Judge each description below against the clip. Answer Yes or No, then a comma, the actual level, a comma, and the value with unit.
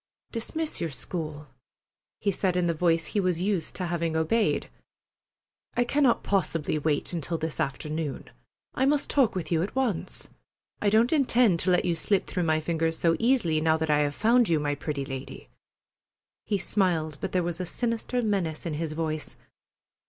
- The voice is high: No, medium, 170 Hz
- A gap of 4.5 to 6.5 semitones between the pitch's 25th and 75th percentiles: Yes, average, 4.8 semitones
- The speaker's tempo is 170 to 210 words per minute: Yes, average, 180 wpm